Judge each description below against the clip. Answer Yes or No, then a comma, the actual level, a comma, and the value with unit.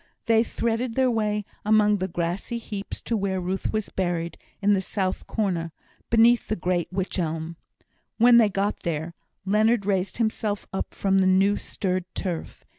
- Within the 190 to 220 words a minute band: No, average, 165 wpm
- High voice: Yes, high, 200 Hz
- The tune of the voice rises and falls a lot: No, average, 3.0 semitones